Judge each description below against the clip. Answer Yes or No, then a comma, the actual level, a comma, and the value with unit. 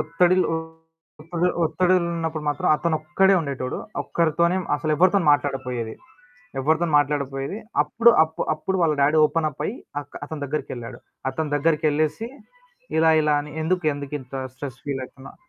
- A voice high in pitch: No, medium, 155 Hz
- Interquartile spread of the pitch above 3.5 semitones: No, average, 2.9 semitones